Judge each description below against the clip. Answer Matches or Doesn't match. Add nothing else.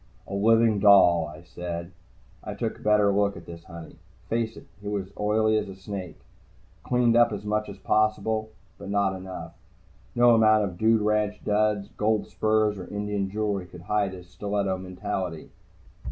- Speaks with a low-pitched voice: Matches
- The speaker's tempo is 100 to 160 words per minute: Doesn't match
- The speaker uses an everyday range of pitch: Doesn't match